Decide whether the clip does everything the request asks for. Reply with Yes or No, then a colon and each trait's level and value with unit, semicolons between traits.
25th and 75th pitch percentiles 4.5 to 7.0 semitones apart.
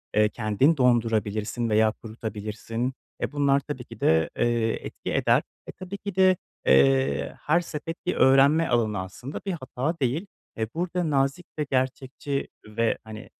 Yes: wide, 5.5 semitones